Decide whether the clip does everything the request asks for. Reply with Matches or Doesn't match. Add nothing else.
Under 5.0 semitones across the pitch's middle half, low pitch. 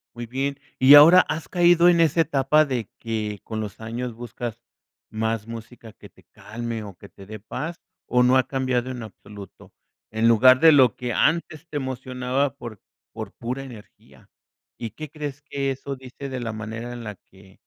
Matches